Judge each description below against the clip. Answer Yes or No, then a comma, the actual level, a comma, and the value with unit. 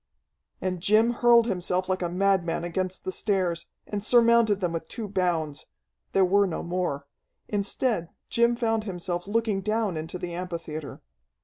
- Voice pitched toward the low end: No, medium, 185 Hz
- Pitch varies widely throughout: No, average, 3.7 semitones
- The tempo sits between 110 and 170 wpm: Yes, average, 150 wpm